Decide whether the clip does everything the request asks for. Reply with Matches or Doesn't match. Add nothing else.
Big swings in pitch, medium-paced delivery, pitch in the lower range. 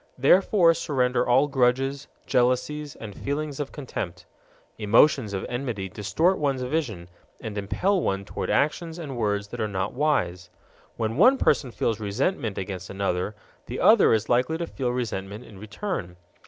Matches